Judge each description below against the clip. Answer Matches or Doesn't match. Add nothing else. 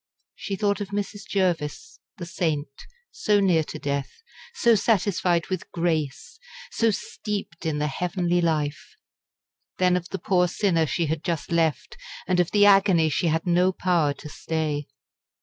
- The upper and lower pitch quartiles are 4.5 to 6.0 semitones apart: Doesn't match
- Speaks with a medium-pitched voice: Matches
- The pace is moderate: Matches